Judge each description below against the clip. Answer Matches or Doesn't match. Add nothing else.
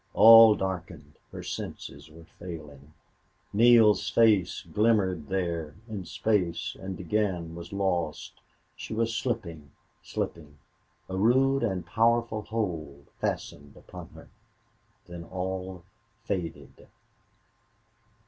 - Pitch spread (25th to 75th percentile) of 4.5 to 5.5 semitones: Matches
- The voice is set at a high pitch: Doesn't match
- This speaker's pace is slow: Matches